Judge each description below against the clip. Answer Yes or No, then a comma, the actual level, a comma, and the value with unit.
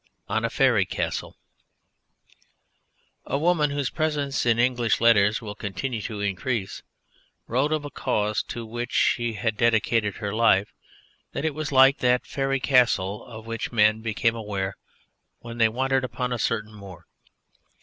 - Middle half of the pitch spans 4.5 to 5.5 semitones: No, average, 3.7 semitones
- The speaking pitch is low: Yes, low, 115 Hz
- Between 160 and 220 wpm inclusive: No, average, 150 wpm